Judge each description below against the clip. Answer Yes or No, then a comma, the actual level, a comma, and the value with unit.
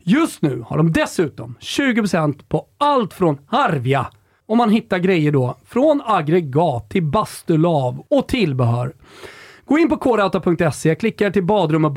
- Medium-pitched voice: Yes, medium, 180 Hz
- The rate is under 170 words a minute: Yes, average, 150 wpm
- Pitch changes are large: Yes, wide, 7.7 semitones